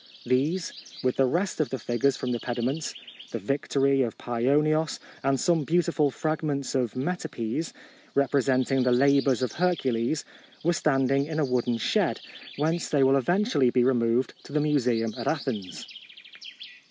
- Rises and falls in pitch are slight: No, average, 3.5 semitones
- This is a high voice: No, low, 135 Hz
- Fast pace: No, average, 155 wpm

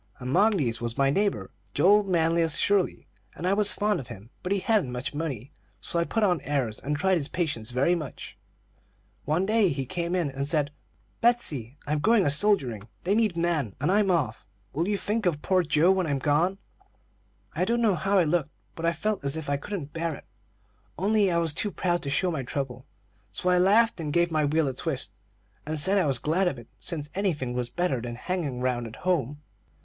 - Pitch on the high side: No, medium, 165 Hz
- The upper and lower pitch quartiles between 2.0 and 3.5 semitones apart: No, average, 5.3 semitones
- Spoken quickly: Yes, fast, 215 wpm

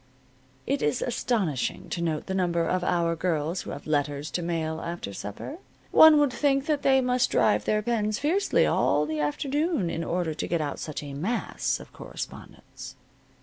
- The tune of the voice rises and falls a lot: Yes, wide, 8.2 semitones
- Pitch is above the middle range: No, medium, 175 Hz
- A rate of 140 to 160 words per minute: No, average, 180 wpm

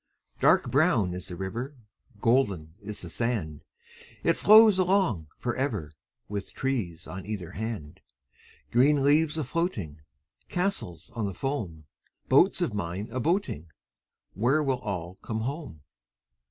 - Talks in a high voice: No, low, 110 Hz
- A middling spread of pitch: No, wide, 7.9 semitones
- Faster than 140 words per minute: No, slow, 135 wpm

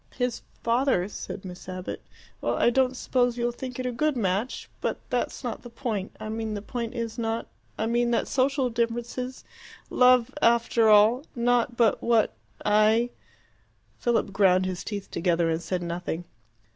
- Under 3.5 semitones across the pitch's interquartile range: Yes, average, 3.1 semitones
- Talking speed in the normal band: Yes, average, 170 wpm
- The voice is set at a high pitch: Yes, high, 230 Hz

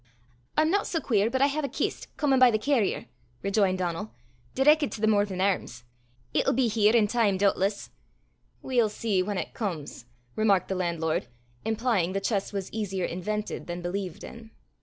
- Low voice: No, high, 210 Hz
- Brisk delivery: No, average, 175 wpm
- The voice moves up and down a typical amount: Yes, average, 4.0 semitones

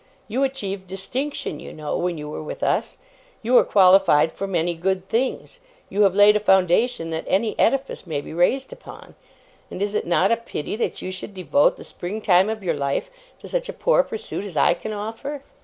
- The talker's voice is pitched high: Yes, high, 195 Hz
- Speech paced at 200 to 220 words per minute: Yes, fast, 205 wpm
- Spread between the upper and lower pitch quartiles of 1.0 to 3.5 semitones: No, average, 4.8 semitones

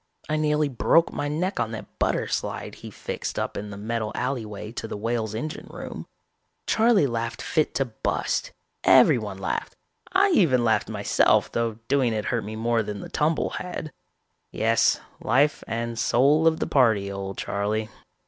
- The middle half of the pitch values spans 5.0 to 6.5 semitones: Yes, wide, 5.5 semitones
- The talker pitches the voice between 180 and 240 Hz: No, low, 115 Hz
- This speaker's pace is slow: No, average, 165 wpm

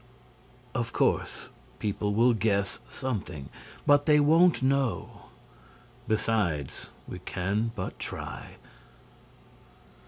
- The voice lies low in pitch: Yes, low, 110 Hz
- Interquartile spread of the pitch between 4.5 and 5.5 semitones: Yes, average, 5.1 semitones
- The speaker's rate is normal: No, slow, 90 wpm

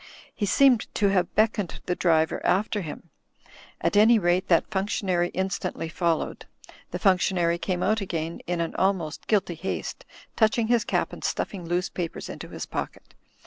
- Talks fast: No, average, 160 wpm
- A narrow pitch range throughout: No, average, 3.2 semitones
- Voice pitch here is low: No, medium, 185 Hz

